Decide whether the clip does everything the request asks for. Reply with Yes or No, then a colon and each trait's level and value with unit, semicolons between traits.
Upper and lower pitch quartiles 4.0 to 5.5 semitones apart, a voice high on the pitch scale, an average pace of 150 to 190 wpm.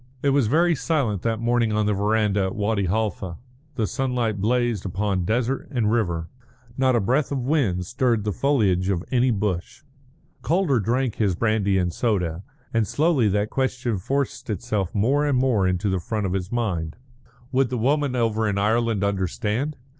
No: average, 4.3 semitones; low, 110 Hz; average, 175 wpm